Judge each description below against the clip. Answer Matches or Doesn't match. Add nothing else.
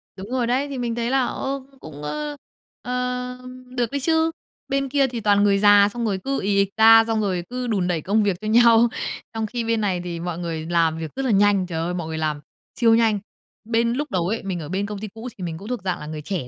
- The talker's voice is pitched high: Matches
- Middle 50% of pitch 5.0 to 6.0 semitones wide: Matches